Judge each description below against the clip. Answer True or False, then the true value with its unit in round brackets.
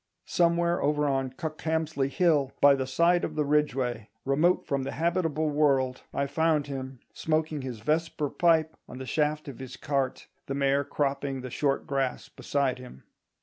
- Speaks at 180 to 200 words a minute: False (165 wpm)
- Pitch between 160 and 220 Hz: False (145 Hz)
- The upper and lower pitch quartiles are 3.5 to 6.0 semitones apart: False (2.8 semitones)